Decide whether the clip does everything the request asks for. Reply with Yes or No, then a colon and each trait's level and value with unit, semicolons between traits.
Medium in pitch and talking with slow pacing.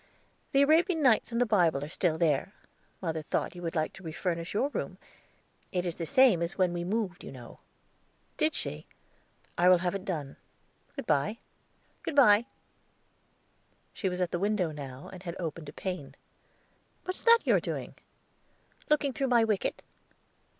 No: medium, 180 Hz; average, 170 wpm